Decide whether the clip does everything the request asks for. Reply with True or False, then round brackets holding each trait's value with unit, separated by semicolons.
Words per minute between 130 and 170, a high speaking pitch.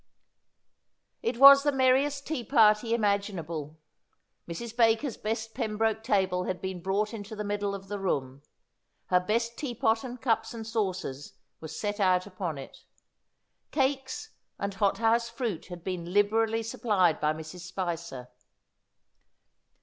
True (140 wpm; 210 Hz)